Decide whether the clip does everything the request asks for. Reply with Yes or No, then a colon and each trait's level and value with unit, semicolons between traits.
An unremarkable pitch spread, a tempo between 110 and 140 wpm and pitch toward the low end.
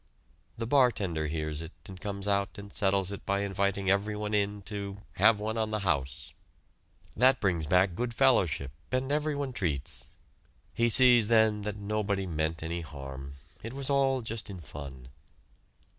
No: average, 4.9 semitones; average, 160 wpm; low, 100 Hz